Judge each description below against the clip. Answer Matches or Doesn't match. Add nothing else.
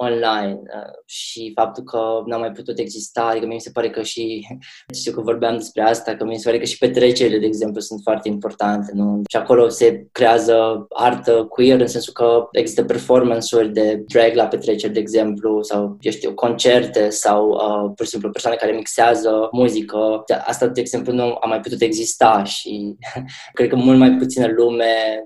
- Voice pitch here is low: Matches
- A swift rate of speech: Matches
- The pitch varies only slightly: Matches